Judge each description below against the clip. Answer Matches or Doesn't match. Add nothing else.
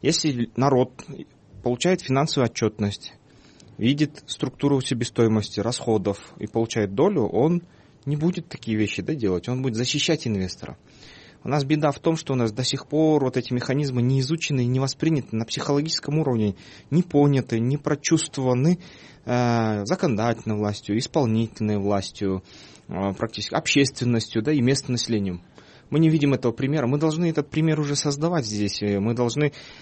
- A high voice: Doesn't match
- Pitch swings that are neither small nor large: Matches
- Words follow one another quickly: Doesn't match